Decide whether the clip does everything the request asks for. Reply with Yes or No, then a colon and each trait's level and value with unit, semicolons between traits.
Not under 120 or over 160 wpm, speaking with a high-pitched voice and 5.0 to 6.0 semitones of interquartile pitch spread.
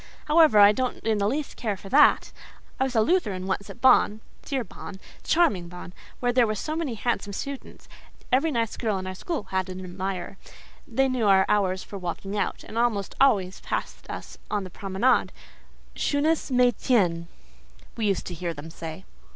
No: average, 175 wpm; high, 210 Hz; average, 5.3 semitones